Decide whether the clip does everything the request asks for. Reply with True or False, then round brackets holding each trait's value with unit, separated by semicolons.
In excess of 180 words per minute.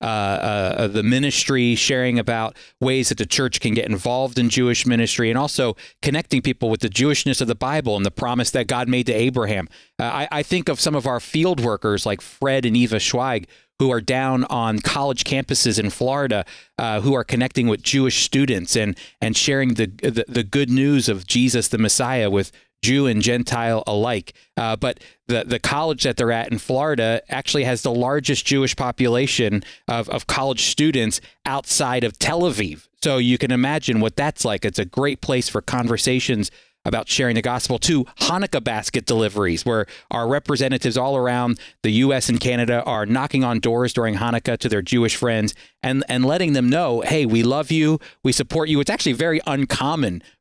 True (190 wpm)